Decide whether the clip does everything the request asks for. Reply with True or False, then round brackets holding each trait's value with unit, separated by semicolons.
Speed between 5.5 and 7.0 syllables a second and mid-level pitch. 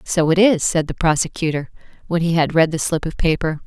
True (5.7 syllables/s; 165 Hz)